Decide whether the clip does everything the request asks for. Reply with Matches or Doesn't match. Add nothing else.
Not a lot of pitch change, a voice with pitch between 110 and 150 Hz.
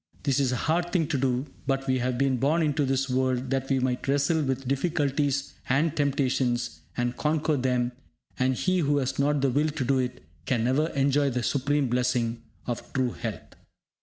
Matches